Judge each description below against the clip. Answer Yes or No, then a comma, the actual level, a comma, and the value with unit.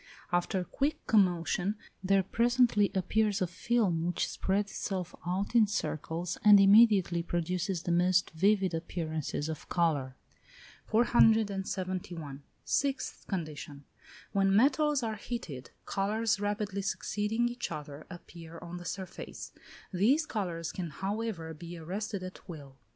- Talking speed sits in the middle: No, slow, 125 wpm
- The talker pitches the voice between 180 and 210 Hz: Yes, high, 190 Hz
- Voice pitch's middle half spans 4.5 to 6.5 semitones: No, average, 3.9 semitones